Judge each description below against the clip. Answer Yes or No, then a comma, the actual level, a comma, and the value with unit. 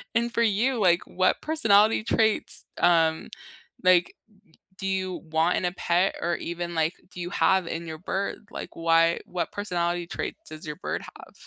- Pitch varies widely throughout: No, average, 2.9 semitones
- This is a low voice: No, medium, 175 Hz